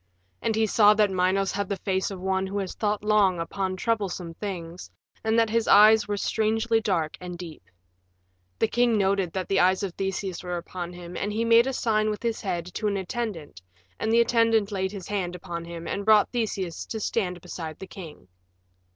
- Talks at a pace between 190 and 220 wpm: Yes, fast, 205 wpm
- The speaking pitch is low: No, high, 195 Hz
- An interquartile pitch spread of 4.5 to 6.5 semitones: No, average, 3.3 semitones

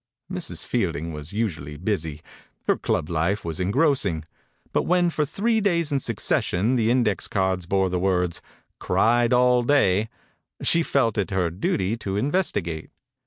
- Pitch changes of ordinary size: No, wide, 6.5 semitones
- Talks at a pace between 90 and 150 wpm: No, average, 160 wpm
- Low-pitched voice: Yes, low, 105 Hz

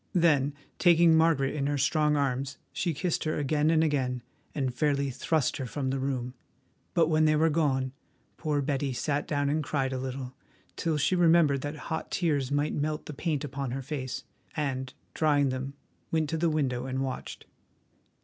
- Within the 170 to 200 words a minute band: Yes, average, 180 wpm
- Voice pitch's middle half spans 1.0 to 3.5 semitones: Yes, average, 2.7 semitones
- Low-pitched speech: No, medium, 145 Hz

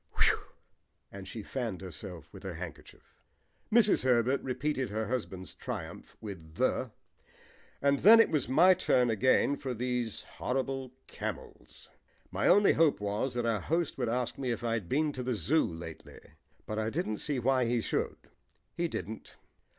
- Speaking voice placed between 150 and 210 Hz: No, low, 125 Hz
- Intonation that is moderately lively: Yes, average, 4.3 semitones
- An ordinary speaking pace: Yes, average, 165 wpm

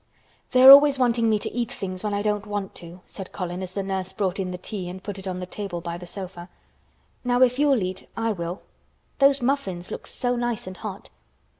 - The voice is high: Yes, high, 200 Hz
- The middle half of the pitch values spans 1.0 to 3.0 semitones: No, average, 4.7 semitones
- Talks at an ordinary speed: No, fast, 230 wpm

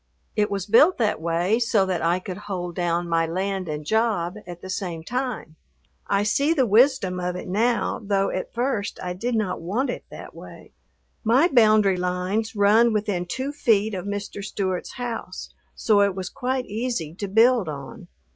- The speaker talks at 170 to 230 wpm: Yes, average, 180 wpm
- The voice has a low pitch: No, high, 200 Hz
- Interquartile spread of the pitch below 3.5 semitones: No, average, 4.1 semitones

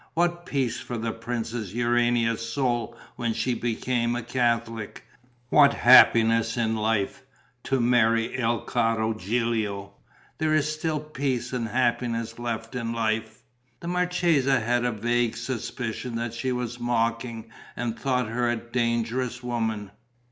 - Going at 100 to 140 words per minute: Yes, slow, 135 wpm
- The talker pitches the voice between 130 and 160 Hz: No, low, 120 Hz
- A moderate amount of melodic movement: No, narrow, 1.7 semitones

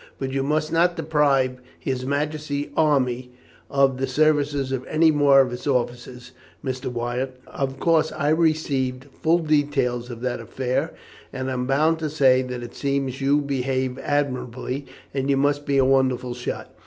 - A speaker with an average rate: Yes, average, 165 wpm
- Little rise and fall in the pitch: Yes, narrow, 2.3 semitones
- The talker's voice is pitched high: No, low, 135 Hz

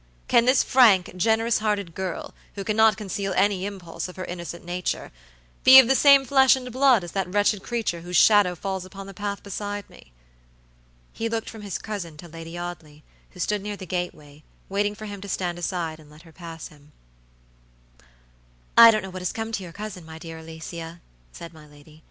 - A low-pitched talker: No, high, 190 Hz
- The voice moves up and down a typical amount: Yes, average, 3.8 semitones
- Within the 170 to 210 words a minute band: Yes, average, 200 wpm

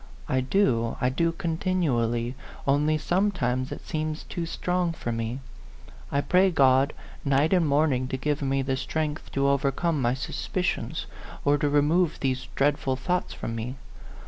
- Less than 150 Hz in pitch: Yes, medium, 140 Hz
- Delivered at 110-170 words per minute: Yes, average, 150 wpm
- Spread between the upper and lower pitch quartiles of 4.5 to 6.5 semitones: No, average, 4.1 semitones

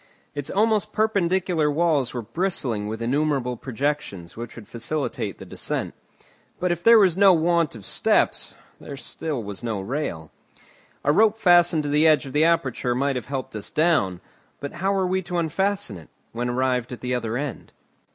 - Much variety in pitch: Yes, wide, 6.1 semitones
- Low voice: No, medium, 145 Hz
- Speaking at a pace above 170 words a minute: Yes, average, 180 wpm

